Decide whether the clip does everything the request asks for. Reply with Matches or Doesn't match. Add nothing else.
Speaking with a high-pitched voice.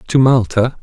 Doesn't match